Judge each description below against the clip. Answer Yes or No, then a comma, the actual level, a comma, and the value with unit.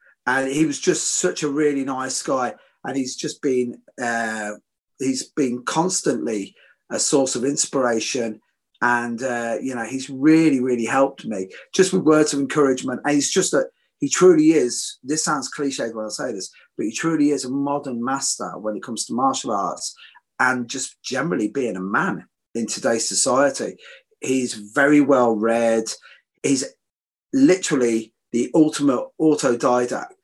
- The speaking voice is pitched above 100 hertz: Yes, low, 135 Hz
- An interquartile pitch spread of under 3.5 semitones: No, average, 4.5 semitones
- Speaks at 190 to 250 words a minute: No, average, 160 wpm